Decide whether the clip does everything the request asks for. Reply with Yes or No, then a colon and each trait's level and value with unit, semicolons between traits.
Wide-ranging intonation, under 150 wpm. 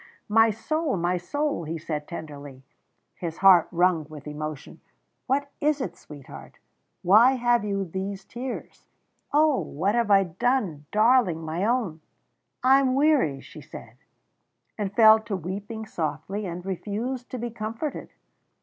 Yes: wide, 6.5 semitones; average, 140 wpm